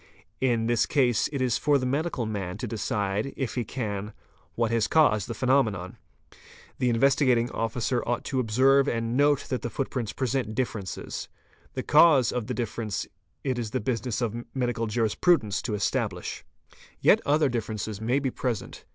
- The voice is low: Yes, low, 120 Hz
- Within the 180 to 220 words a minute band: No, average, 165 wpm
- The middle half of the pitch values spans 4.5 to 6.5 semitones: No, average, 3.2 semitones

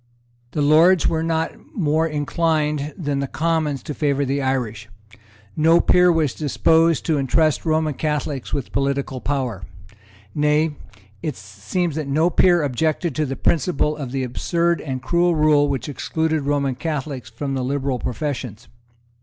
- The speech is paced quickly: No, average, 150 wpm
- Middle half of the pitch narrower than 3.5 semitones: Yes, average, 2.9 semitones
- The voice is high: No, medium, 150 Hz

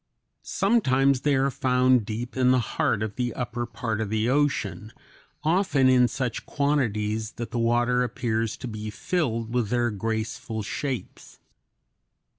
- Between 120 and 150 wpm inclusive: Yes, average, 145 wpm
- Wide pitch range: No, average, 2.8 semitones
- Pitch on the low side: Yes, low, 120 Hz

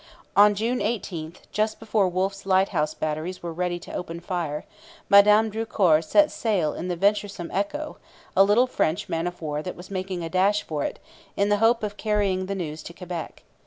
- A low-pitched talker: No, high, 190 Hz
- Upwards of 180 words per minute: Yes, average, 190 wpm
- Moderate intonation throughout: Yes, average, 3.5 semitones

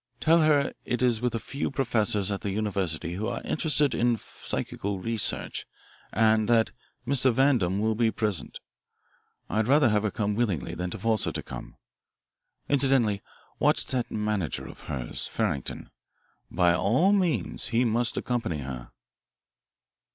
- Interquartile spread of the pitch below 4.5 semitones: Yes, average, 3.9 semitones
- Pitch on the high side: No, low, 110 Hz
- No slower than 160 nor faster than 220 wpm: No, average, 150 wpm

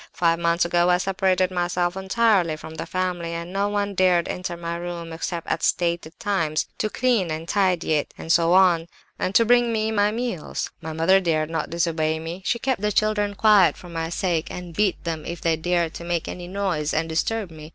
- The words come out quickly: Yes, fast, 210 wpm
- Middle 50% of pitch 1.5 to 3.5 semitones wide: Yes, average, 2.8 semitones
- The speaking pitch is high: No, medium, 175 Hz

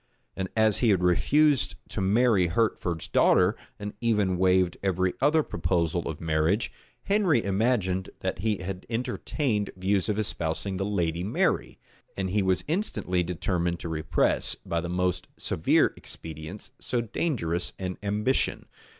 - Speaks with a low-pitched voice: Yes, very low, 95 Hz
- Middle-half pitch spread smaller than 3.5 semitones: No, average, 3.8 semitones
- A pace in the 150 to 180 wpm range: No, average, 140 wpm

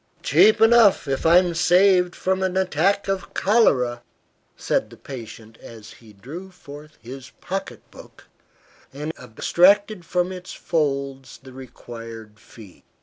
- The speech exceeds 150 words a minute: No, slow, 135 wpm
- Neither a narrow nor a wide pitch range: No, wide, 7.1 semitones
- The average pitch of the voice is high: No, medium, 155 Hz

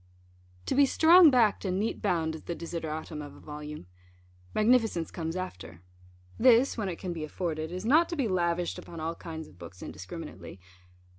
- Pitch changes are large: Yes, wide, 5.8 semitones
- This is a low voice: No, medium, 170 Hz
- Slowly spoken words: No, average, 175 wpm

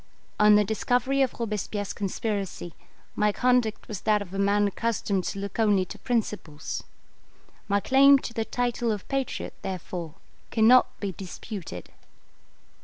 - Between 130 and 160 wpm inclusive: Yes, average, 140 wpm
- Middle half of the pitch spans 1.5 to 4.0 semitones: Yes, average, 3.0 semitones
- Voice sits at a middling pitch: No, high, 210 Hz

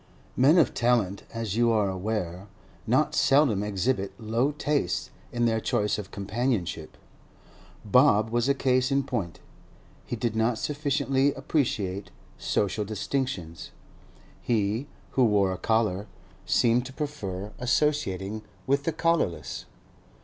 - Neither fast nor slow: No, slow, 125 wpm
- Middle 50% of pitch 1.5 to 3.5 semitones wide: No, average, 4.9 semitones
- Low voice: Yes, low, 115 Hz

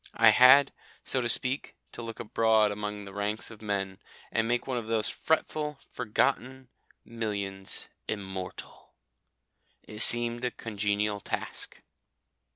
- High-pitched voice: No, low, 110 Hz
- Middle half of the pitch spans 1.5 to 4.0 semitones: Yes, average, 3.0 semitones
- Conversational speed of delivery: No, slow, 130 wpm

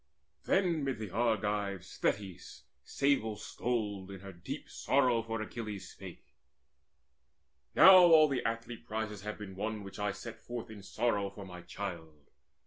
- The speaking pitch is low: Yes, low, 105 Hz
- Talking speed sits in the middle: Yes, average, 145 wpm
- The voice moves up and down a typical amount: Yes, average, 3.3 semitones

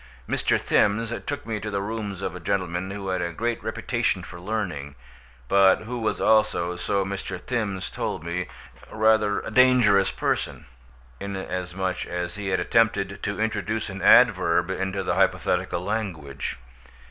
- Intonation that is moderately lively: Yes, average, 3.0 semitones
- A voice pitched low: Yes, low, 100 Hz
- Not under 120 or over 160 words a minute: Yes, average, 150 wpm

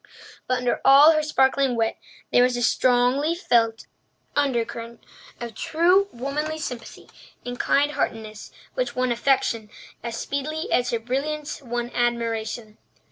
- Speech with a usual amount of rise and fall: Yes, average, 3.7 semitones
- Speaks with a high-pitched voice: Yes, very high, 250 Hz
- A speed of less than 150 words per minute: Yes, slow, 135 wpm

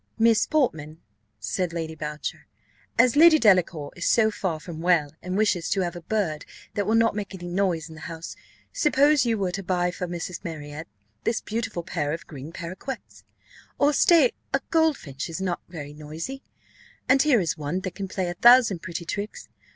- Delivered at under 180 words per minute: No, average, 185 wpm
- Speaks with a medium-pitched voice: Yes, medium, 180 Hz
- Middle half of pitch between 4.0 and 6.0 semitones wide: Yes, wide, 5.6 semitones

